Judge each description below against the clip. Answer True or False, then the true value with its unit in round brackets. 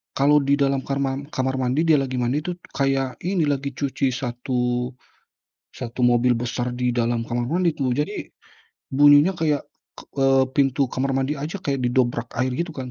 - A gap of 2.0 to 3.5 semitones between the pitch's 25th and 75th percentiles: True (2.5 semitones)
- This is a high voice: False (135 Hz)